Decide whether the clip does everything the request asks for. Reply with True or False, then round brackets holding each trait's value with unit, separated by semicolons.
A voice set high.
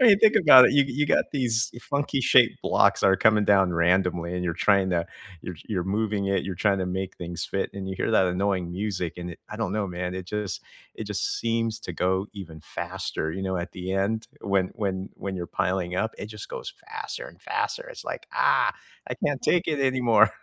False (100 Hz)